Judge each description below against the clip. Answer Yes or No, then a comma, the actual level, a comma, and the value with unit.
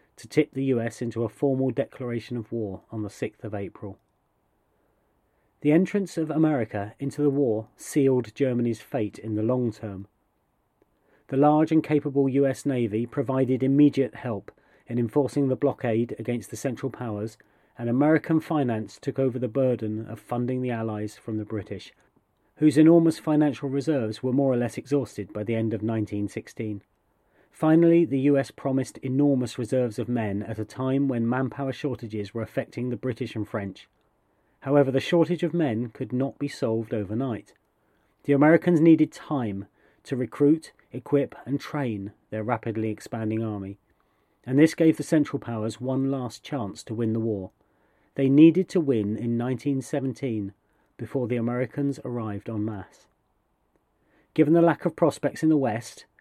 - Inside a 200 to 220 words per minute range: No, average, 160 wpm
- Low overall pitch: Yes, low, 125 Hz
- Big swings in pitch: No, average, 4.3 semitones